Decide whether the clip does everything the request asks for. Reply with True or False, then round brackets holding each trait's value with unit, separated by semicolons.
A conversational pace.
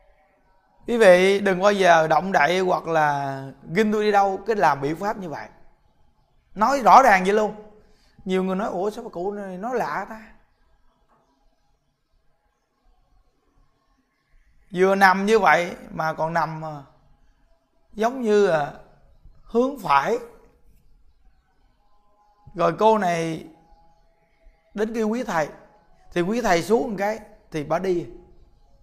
False (130 wpm)